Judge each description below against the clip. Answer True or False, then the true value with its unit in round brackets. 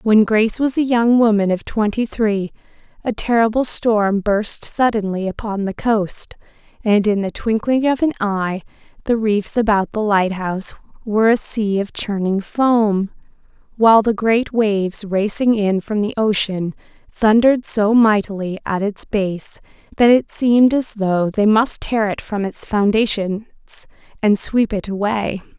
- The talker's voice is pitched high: True (210 Hz)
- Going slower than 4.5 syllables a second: True (4.3 syllables/s)